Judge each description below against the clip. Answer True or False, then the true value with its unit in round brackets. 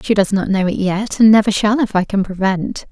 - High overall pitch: True (200 Hz)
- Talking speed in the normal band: False (270 wpm)